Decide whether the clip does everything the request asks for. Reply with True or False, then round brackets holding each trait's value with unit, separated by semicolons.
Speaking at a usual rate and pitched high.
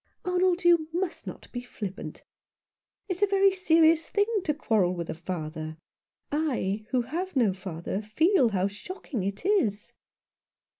True (150 wpm; 255 Hz)